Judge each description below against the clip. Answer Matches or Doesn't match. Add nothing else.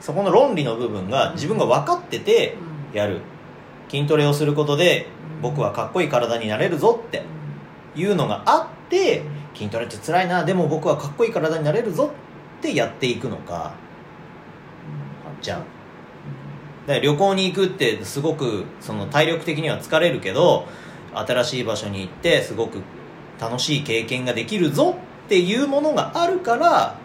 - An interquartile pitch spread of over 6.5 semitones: Matches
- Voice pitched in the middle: Matches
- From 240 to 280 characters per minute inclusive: Doesn't match